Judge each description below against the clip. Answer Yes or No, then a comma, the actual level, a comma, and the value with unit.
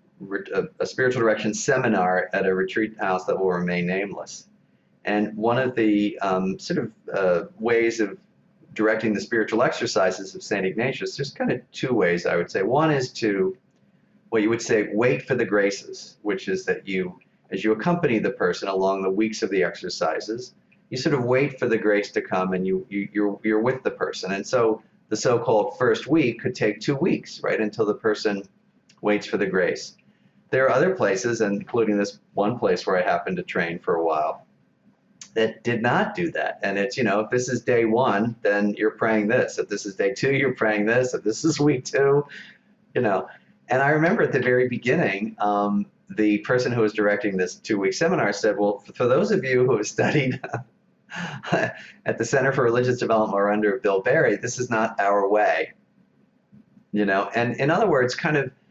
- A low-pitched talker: Yes, low, 110 Hz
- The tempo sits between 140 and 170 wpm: No, average, 200 wpm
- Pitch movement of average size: Yes, average, 3.6 semitones